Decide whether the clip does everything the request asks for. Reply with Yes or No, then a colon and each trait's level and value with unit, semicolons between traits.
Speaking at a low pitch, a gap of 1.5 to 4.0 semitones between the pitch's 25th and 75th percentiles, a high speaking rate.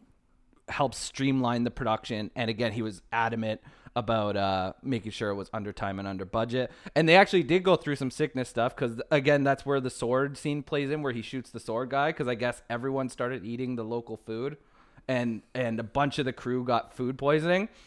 Yes: low, 125 Hz; average, 3.5 semitones; fast, 210 wpm